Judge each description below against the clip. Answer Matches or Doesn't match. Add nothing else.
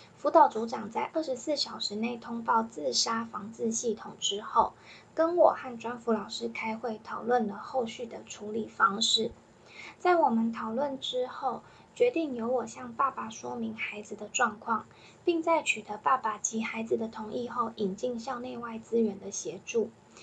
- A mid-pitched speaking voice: Doesn't match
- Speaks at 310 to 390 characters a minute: Doesn't match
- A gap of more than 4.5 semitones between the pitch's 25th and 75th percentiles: Doesn't match